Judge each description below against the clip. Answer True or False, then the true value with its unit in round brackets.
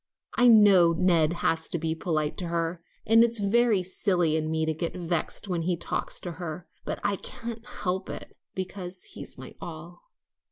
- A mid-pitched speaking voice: True (180 Hz)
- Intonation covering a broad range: False (3.6 semitones)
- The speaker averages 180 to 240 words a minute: True (185 wpm)